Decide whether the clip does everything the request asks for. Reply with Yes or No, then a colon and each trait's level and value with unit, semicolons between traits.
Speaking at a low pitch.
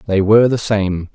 Yes: low, 105 Hz